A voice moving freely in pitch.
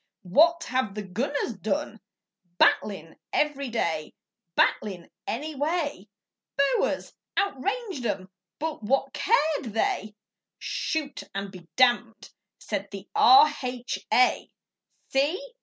Yes: wide, 6.4 semitones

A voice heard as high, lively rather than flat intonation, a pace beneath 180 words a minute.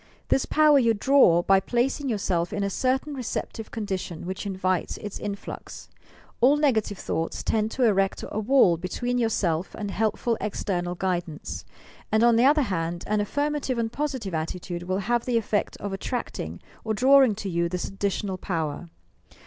No: high, 205 Hz; average, 5.0 semitones; average, 165 wpm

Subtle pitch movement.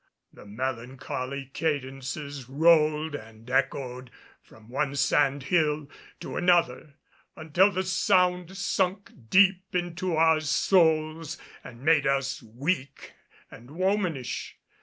No: average, 4.7 semitones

